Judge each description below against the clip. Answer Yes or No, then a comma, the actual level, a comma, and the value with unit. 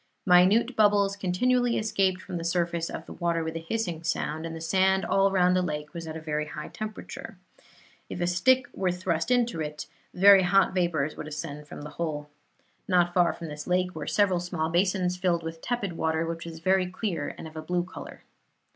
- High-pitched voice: No, medium, 175 Hz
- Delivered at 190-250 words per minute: Yes, average, 200 wpm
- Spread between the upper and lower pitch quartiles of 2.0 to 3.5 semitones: Yes, average, 2.8 semitones